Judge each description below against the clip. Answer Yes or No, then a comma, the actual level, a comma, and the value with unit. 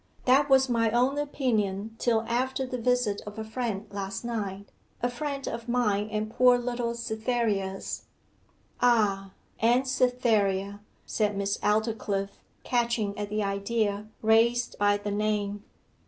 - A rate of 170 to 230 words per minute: No, slow, 135 wpm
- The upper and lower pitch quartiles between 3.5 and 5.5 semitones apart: No, average, 3.1 semitones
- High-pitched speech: Yes, high, 220 Hz